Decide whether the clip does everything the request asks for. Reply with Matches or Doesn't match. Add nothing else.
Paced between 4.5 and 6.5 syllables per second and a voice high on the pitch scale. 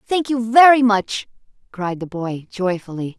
Doesn't match